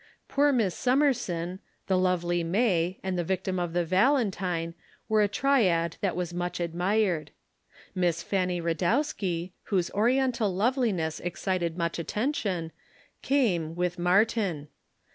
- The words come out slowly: Yes, slow, 125 wpm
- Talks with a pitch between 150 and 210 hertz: Yes, medium, 185 Hz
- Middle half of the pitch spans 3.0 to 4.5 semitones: Yes, average, 4.1 semitones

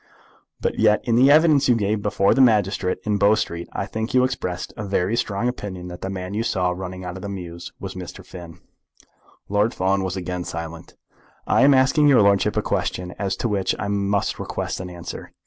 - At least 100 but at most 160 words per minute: No, fast, 205 wpm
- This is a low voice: Yes, low, 100 Hz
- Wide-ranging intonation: No, average, 3.4 semitones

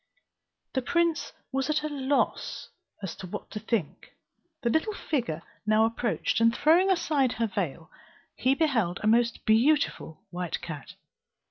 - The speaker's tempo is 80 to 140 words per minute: Yes, slow, 135 wpm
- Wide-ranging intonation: Yes, wide, 5.9 semitones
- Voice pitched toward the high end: Yes, high, 235 Hz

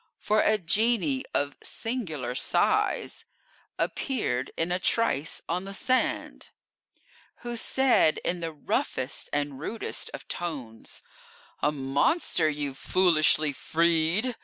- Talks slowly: Yes, slow, 110 wpm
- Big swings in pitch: Yes, wide, 7.1 semitones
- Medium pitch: Yes, medium, 165 Hz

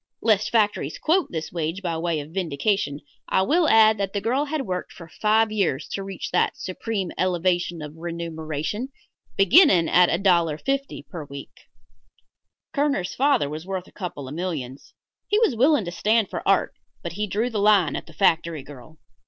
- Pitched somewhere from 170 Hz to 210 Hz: Yes, medium, 185 Hz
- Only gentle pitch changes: No, average, 4.9 semitones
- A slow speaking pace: No, average, 175 wpm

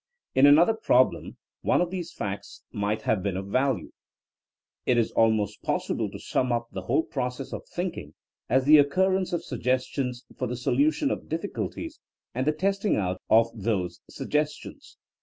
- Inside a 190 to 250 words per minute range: No, average, 170 wpm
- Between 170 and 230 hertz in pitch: No, low, 130 Hz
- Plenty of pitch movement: Yes, wide, 7.0 semitones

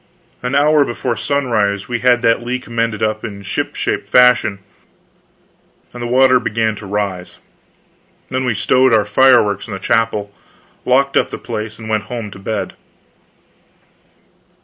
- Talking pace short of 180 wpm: Yes, average, 150 wpm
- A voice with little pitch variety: No, average, 3.2 semitones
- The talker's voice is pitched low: Yes, low, 115 Hz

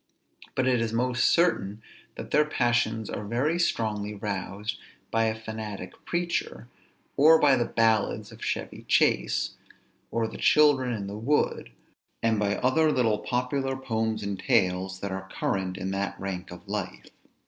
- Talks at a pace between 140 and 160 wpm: Yes, average, 155 wpm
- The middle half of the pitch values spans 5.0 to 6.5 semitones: No, average, 4.2 semitones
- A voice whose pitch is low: Yes, low, 110 Hz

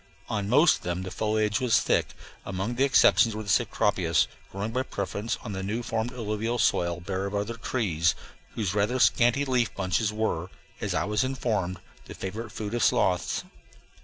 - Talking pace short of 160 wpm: No, average, 175 wpm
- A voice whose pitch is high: No, low, 105 Hz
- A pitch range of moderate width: Yes, average, 3.5 semitones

